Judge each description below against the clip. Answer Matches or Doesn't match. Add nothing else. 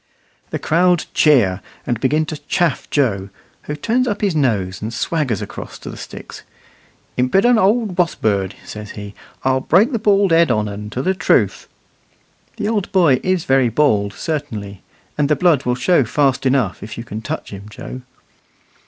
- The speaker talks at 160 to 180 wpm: Matches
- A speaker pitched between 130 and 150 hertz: Matches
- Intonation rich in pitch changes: Matches